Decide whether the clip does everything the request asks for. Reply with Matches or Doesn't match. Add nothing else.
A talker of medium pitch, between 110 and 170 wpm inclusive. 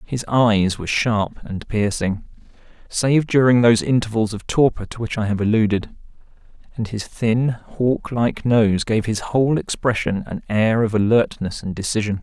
Doesn't match